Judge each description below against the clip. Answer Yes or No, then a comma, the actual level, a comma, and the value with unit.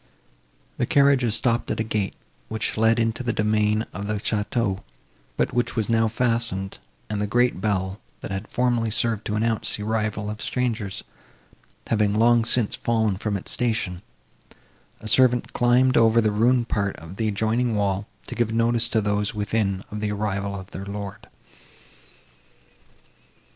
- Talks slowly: No, average, 160 wpm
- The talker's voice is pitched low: Yes, low, 110 Hz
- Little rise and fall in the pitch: Yes, narrow, 2.2 semitones